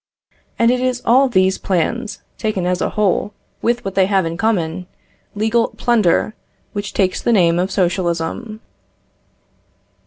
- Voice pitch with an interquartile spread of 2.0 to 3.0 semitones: No, average, 4.1 semitones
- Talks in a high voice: Yes, high, 200 Hz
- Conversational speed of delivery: Yes, average, 145 wpm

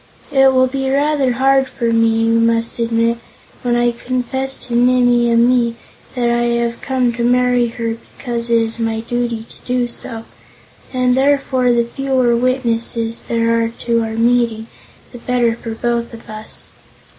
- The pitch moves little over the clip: Yes, narrow, 1.5 semitones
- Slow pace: No, average, 165 wpm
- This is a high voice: Yes, high, 240 Hz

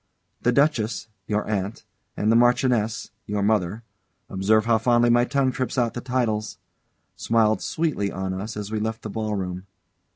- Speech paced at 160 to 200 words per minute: Yes, average, 165 wpm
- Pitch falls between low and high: No, low, 110 Hz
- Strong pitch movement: No, narrow, 2.6 semitones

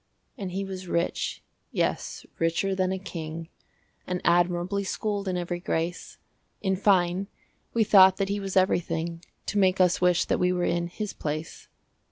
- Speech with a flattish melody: Yes, narrow, 2.0 semitones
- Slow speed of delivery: No, average, 165 wpm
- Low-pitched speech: No, medium, 180 Hz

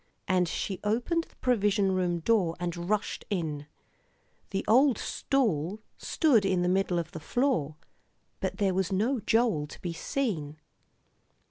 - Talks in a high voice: Yes, high, 195 Hz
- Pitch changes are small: No, average, 4.7 semitones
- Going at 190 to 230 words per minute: No, average, 145 wpm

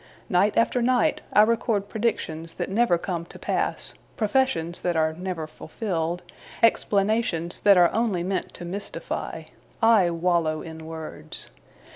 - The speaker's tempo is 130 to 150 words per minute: Yes, slow, 135 wpm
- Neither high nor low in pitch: Yes, medium, 180 Hz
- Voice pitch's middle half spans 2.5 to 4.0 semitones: No, average, 4.7 semitones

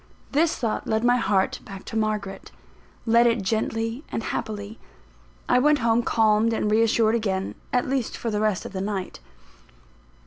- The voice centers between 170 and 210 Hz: No, high, 220 Hz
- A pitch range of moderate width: No, narrow, 1.9 semitones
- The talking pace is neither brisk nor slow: Yes, average, 165 wpm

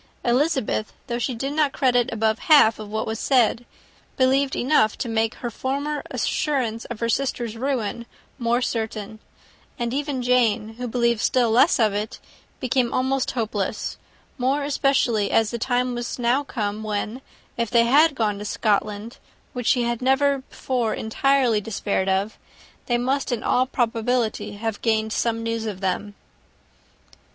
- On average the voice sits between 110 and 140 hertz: No, high, 235 Hz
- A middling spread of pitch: Yes, average, 3.0 semitones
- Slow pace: No, average, 160 wpm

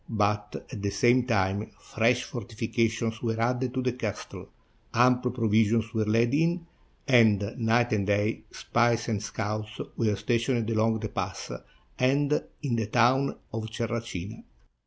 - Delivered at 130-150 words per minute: Yes, average, 140 wpm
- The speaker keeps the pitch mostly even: Yes, narrow, 2.3 semitones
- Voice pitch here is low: Yes, low, 115 Hz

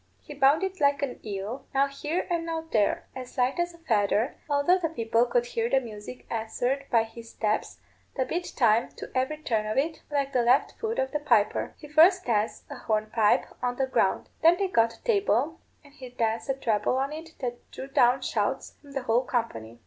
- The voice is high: Yes, very high, 260 Hz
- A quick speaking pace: Yes, fast, 210 wpm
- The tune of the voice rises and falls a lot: No, average, 4.6 semitones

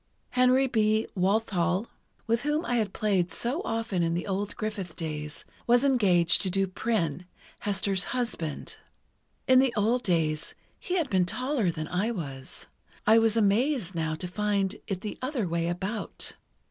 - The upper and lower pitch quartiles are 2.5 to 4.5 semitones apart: No, average, 5.0 semitones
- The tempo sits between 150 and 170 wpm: Yes, average, 160 wpm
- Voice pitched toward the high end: Yes, high, 205 Hz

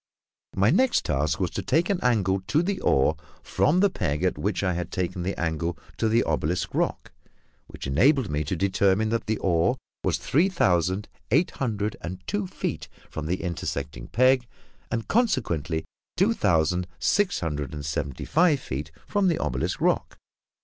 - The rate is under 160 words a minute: No, average, 170 wpm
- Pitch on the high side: No, very low, 95 Hz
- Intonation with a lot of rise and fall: Yes, wide, 8.7 semitones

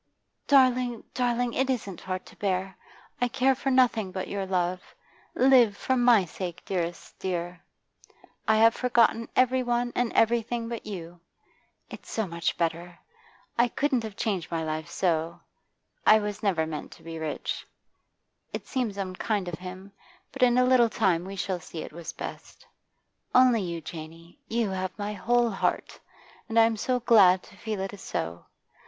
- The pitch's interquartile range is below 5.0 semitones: No, average, 5.3 semitones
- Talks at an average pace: Yes, average, 165 wpm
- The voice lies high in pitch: Yes, high, 205 Hz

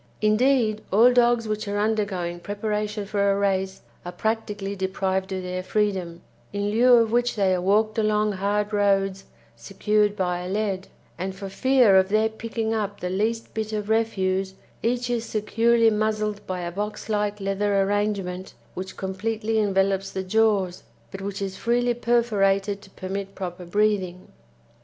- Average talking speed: Yes, average, 160 wpm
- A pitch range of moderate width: No, narrow, 2.2 semitones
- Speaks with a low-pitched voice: No, high, 205 Hz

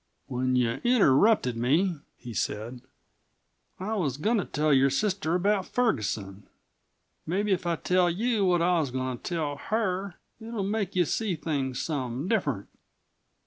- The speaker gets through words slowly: No, average, 150 wpm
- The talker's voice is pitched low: No, medium, 170 Hz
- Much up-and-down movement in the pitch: Yes, wide, 7.2 semitones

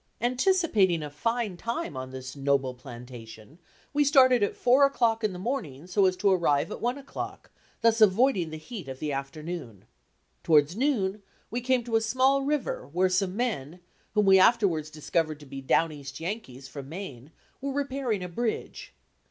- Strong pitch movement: Yes, wide, 8.7 semitones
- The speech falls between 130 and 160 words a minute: No, average, 175 wpm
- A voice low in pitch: No, medium, 185 Hz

